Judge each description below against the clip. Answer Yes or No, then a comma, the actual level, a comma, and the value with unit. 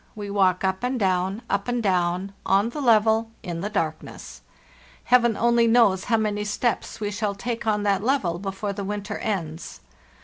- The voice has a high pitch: Yes, high, 205 Hz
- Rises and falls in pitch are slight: No, average, 3.0 semitones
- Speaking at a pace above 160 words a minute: Yes, average, 175 wpm